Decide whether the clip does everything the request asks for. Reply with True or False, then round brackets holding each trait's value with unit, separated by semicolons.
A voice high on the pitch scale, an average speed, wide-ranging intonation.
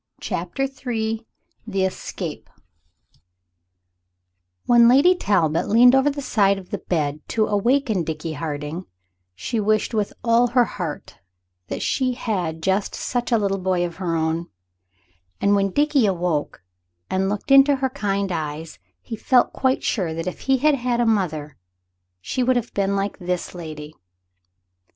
True (200 Hz; 155 wpm; 6.1 semitones)